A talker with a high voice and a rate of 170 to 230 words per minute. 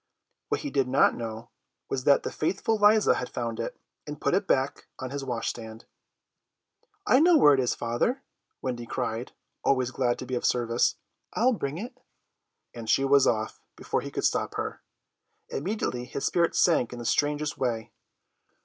No: low, 135 Hz; average, 175 wpm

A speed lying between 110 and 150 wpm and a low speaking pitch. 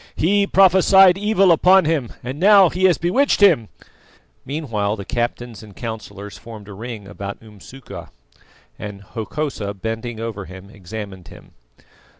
Yes: average, 140 wpm; low, 115 Hz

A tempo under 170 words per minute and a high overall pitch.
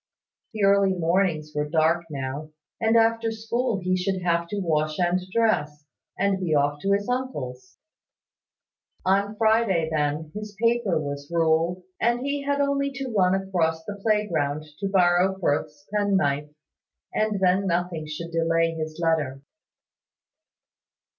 No: average, 140 wpm; medium, 180 Hz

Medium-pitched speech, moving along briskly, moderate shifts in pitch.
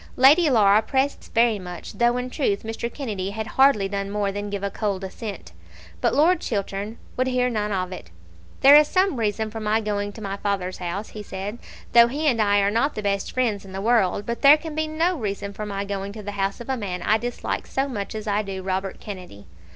No: high, 210 Hz; fast, 235 wpm; average, 3.7 semitones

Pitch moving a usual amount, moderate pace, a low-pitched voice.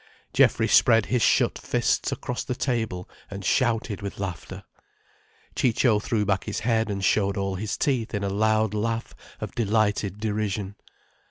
No: narrow, 2.2 semitones; average, 155 wpm; low, 105 Hz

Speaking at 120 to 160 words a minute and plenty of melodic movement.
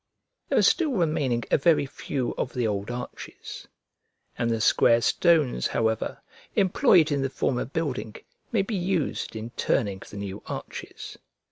Yes: average, 150 wpm; wide, 6.6 semitones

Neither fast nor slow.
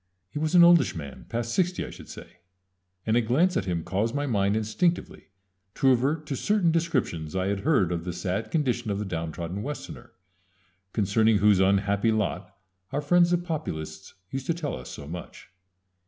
Yes: average, 185 wpm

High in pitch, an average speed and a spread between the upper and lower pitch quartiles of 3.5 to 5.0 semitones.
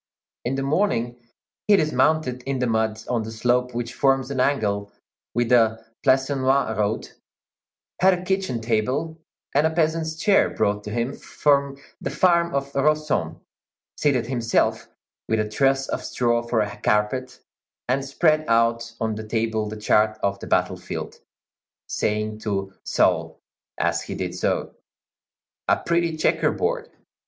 No: low, 125 Hz; average, 150 wpm; average, 4.6 semitones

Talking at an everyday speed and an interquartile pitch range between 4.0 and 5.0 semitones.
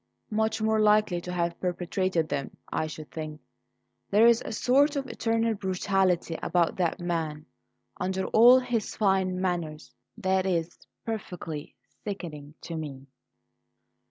No: slow, 130 wpm; average, 4.7 semitones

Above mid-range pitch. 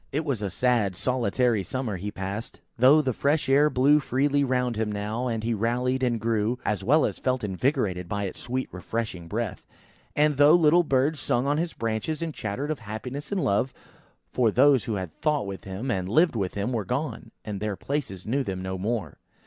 No: low, 120 Hz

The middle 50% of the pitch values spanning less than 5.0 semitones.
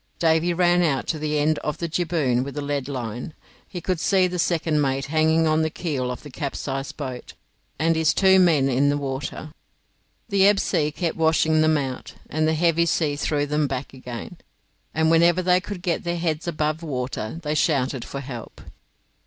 Yes: average, 3.2 semitones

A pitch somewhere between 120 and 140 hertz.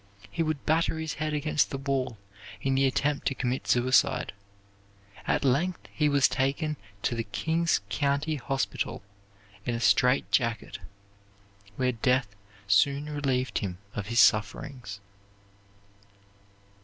Yes: low, 135 Hz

